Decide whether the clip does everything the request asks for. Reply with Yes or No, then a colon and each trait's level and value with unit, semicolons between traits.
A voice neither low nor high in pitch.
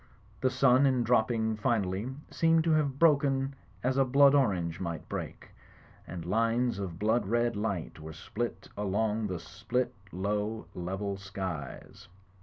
No: low, 110 Hz